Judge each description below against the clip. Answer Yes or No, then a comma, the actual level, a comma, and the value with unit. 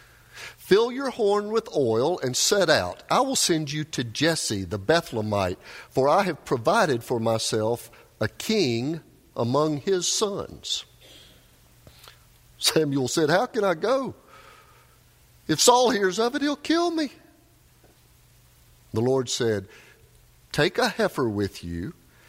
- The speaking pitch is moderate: Yes, medium, 155 Hz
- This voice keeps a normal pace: No, slow, 130 wpm